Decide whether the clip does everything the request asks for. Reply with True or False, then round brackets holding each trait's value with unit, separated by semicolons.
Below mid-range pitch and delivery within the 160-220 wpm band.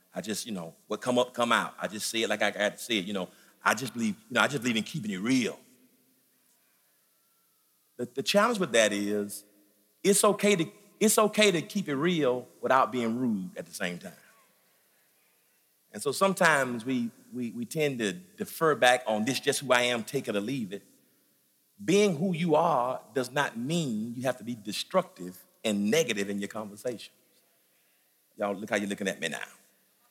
True (130 Hz; 200 wpm)